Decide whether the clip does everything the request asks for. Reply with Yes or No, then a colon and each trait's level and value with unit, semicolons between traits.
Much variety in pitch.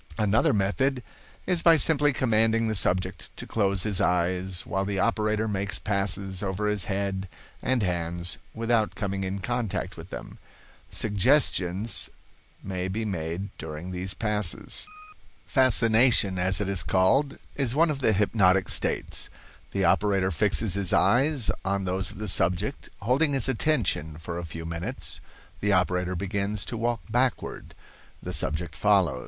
No: average, 3.5 semitones